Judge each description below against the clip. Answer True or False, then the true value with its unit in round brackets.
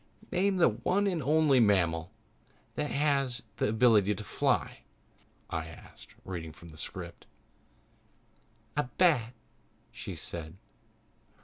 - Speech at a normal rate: False (115 wpm)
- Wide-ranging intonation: True (8.6 semitones)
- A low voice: True (120 Hz)